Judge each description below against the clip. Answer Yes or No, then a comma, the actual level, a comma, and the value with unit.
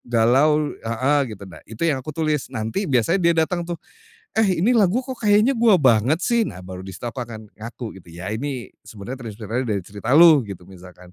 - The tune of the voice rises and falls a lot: Yes, wide, 7.4 semitones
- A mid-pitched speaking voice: No, low, 125 Hz